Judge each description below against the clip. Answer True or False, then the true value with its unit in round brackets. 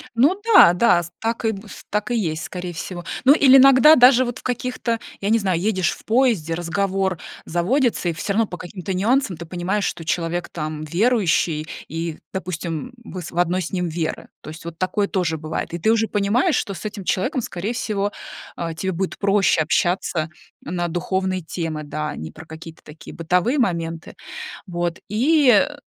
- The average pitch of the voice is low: False (185 Hz)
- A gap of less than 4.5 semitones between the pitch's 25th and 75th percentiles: False (5.1 semitones)